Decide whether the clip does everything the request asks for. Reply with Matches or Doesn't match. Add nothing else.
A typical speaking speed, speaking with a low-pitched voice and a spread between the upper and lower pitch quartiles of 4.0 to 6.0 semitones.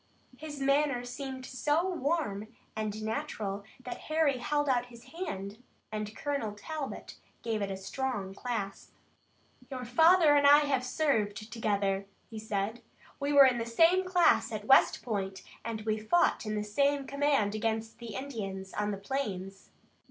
Doesn't match